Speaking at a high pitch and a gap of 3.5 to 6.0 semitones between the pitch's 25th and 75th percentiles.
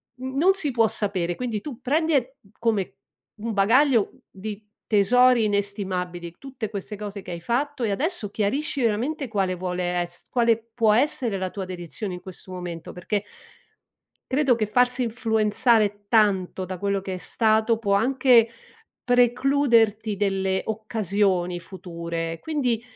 Yes: high, 215 Hz; average, 4.4 semitones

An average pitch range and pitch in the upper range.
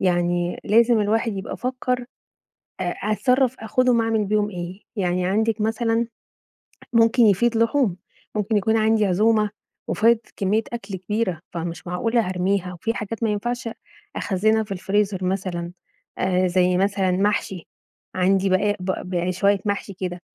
Yes: average, 3.6 semitones; high, 205 Hz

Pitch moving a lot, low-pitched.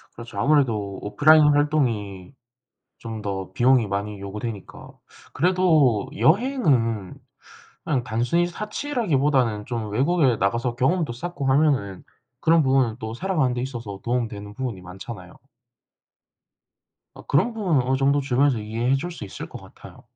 Yes: wide, 6.0 semitones; low, 125 Hz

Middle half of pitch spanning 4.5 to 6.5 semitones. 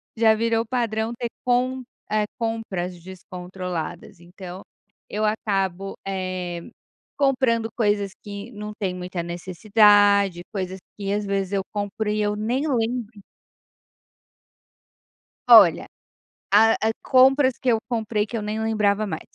No: average, 3.0 semitones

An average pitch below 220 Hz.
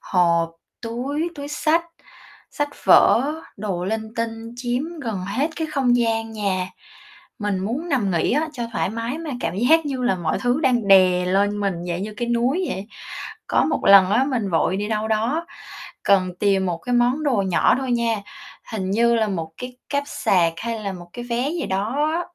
No: high, 225 Hz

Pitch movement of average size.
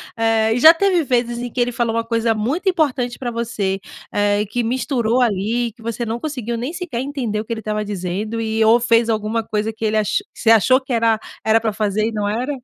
No: narrow, 2.1 semitones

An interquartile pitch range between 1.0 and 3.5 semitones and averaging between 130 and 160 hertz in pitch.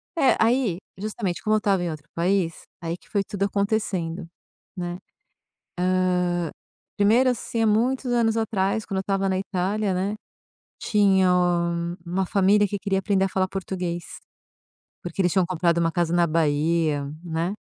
No: average, 3.1 semitones; high, 190 Hz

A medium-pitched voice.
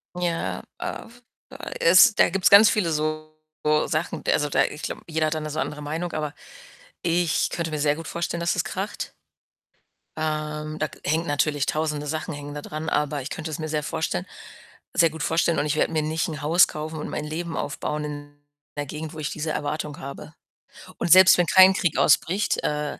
Yes: medium, 155 Hz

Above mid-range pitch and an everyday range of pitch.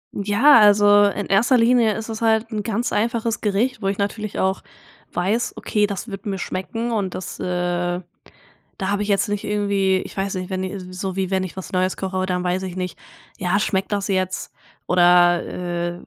No: high, 195 Hz; narrow, 2.3 semitones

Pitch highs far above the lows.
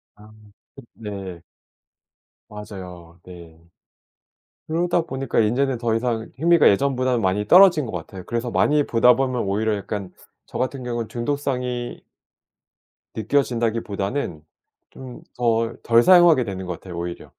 No: average, 4.9 semitones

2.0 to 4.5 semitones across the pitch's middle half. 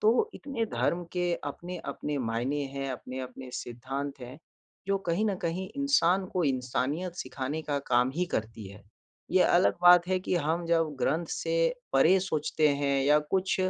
No: wide, 5.5 semitones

